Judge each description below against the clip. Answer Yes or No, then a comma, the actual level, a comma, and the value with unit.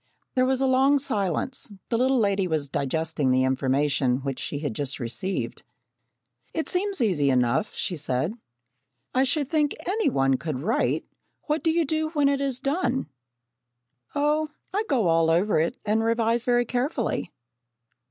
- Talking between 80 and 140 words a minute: No, average, 160 wpm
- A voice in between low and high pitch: No, high, 220 Hz